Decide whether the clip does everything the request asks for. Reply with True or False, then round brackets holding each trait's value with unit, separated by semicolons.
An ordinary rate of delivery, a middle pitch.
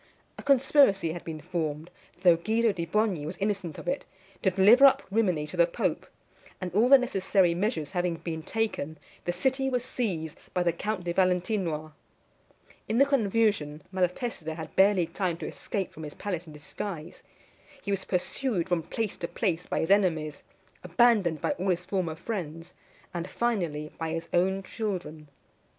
True (170 wpm; 180 Hz)